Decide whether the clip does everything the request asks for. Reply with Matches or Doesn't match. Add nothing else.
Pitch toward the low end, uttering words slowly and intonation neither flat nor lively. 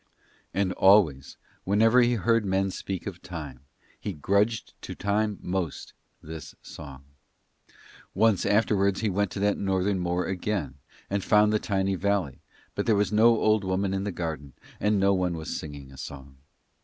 Doesn't match